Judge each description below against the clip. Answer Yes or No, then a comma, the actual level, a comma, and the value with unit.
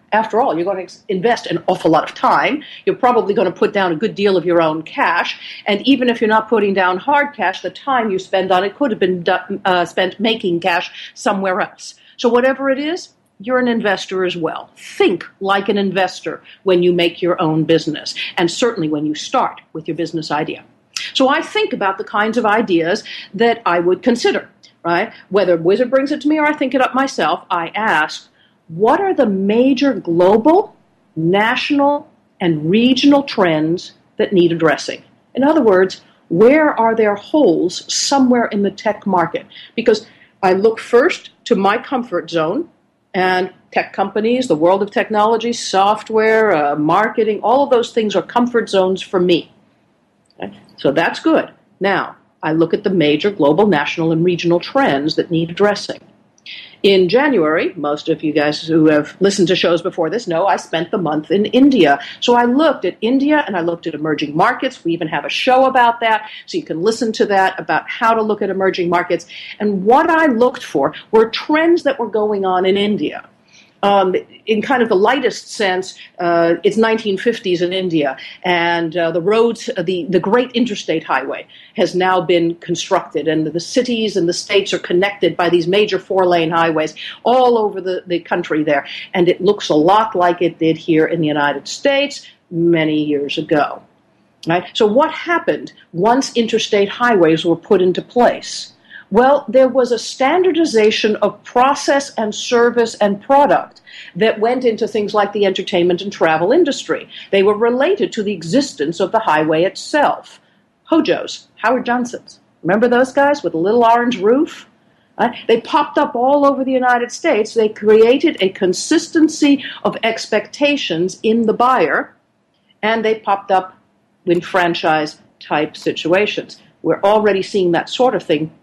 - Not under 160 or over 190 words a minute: Yes, average, 180 wpm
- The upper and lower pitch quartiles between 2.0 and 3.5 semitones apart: No, wide, 5.5 semitones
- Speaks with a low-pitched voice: No, high, 205 Hz